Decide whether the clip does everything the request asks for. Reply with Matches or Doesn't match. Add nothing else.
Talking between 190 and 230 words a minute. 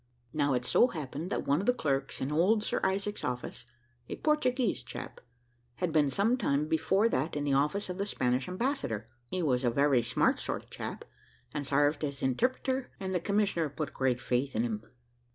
Matches